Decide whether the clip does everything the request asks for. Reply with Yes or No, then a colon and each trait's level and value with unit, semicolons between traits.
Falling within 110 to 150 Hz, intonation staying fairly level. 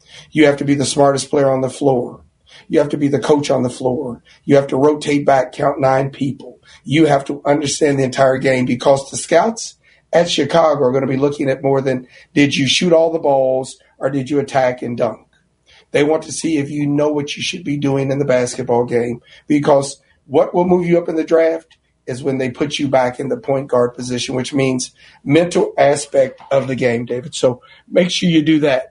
Yes: medium, 140 Hz; narrow, 2.3 semitones